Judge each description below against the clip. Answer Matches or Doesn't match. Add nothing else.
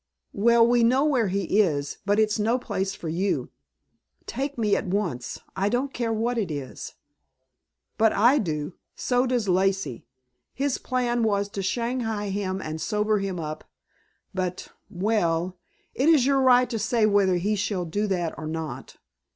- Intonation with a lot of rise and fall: Doesn't match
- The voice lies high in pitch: Matches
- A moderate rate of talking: Matches